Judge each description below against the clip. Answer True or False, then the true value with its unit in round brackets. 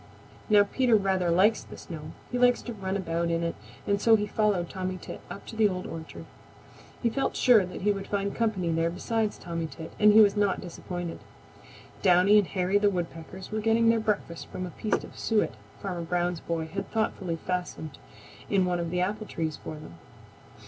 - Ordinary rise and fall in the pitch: True (3.7 semitones)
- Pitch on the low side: False (190 Hz)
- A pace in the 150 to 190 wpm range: False (200 wpm)